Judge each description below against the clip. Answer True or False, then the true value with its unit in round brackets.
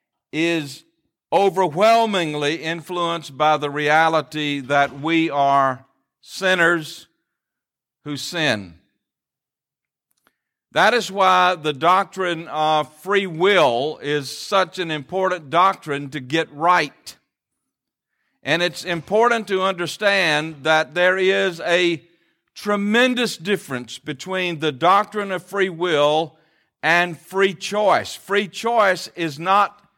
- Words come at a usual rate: False (105 wpm)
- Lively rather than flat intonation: False (3.8 semitones)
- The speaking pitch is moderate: True (170 Hz)